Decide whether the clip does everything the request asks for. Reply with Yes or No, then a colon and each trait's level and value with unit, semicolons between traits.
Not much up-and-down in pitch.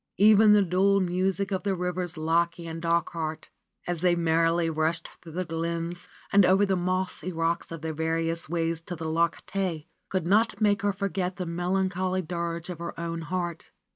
Yes: narrow, 2.1 semitones